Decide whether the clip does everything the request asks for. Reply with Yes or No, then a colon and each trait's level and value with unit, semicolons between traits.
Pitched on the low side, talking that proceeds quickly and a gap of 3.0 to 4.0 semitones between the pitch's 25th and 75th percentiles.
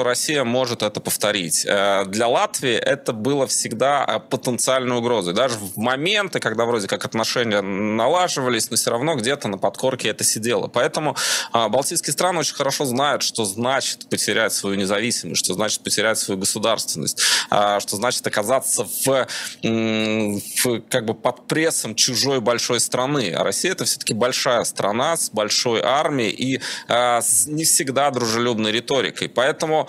No: low, 120 Hz; average, 150 wpm; average, 3.5 semitones